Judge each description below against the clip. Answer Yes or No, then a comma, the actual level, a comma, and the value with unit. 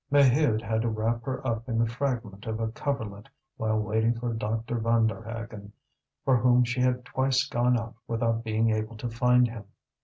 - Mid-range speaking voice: No, low, 115 Hz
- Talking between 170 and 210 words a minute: Yes, average, 180 wpm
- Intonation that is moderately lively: No, narrow, 1.9 semitones